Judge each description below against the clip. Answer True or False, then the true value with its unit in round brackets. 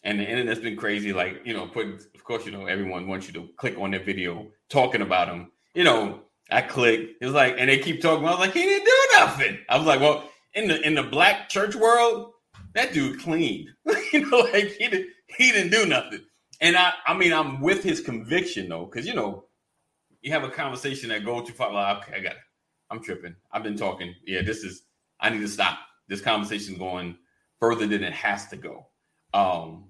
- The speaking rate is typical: False (225 wpm)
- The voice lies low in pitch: True (125 Hz)